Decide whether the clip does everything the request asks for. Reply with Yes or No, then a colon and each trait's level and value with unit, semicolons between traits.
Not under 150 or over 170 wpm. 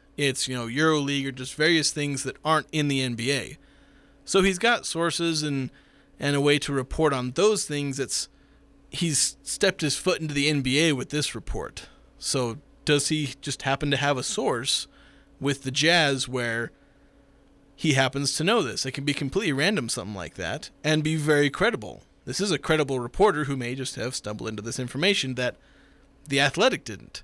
No: average, 185 wpm